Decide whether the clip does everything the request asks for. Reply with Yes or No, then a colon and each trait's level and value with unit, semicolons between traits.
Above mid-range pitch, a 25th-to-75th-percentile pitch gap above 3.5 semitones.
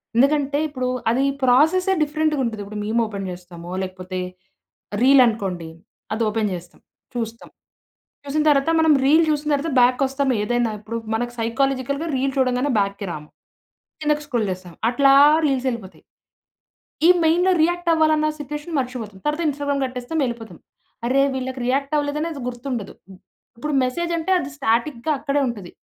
Yes: very high, 260 Hz; average, 4.7 semitones